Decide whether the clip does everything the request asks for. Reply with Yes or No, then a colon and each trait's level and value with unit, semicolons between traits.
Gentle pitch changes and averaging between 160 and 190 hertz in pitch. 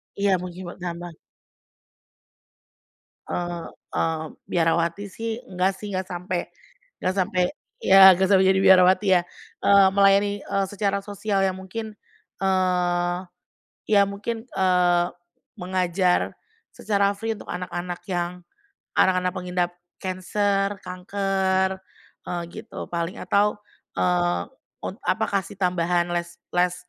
Yes: narrow, 1.9 semitones; medium, 185 Hz